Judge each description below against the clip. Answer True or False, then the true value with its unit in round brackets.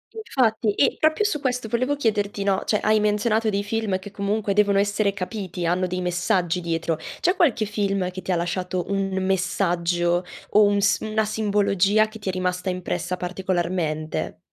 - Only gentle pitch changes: False (3.0 semitones)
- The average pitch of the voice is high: True (200 Hz)